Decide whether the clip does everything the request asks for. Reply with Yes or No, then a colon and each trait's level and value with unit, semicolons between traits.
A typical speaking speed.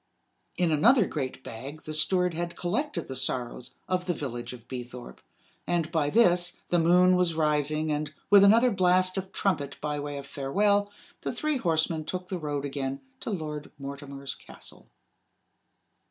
Yes: average, 160 wpm